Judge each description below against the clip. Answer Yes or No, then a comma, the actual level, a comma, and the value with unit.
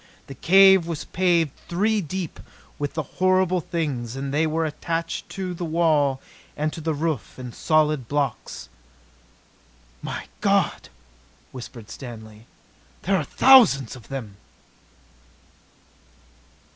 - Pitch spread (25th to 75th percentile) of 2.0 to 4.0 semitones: No, average, 4.5 semitones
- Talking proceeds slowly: Yes, slow, 115 wpm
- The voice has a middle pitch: Yes, medium, 155 Hz